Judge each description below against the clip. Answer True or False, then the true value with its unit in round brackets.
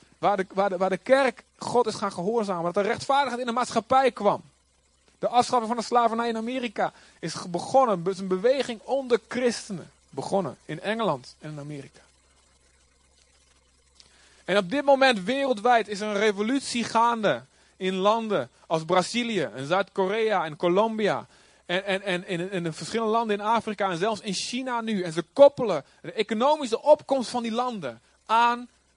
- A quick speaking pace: False (170 wpm)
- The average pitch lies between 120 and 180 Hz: False (210 Hz)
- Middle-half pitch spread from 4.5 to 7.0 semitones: True (5.1 semitones)